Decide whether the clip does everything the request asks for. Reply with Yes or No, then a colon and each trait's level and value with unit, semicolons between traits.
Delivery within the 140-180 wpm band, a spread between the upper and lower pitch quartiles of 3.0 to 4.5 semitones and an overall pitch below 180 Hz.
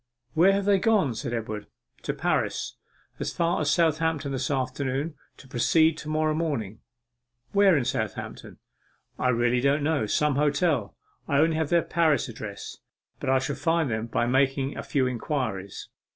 Yes: average, 165 wpm; average, 4.2 semitones; medium, 140 Hz